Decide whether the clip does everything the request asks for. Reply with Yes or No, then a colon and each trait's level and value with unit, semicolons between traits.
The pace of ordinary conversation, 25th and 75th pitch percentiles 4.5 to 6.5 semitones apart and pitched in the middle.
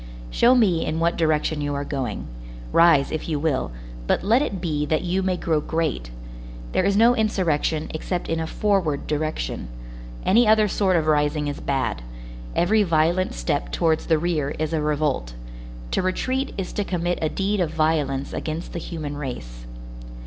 No: average, 175 wpm; average, 3.9 semitones; medium, 160 Hz